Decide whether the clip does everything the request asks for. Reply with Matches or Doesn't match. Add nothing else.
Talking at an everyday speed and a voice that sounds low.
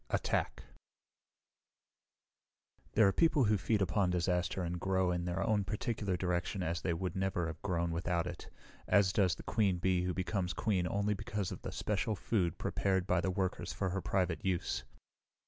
Matches